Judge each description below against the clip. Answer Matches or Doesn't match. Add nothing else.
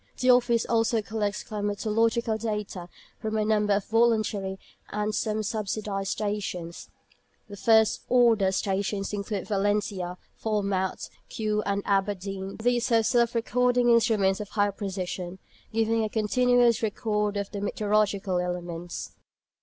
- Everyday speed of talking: Doesn't match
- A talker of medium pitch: Doesn't match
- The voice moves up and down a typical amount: Doesn't match